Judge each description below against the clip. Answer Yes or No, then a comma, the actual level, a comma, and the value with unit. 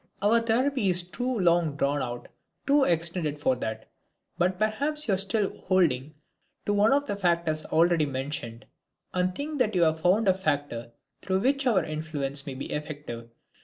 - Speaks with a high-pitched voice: No, medium, 175 Hz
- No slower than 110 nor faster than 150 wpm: No, average, 170 wpm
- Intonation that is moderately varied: No, wide, 6.5 semitones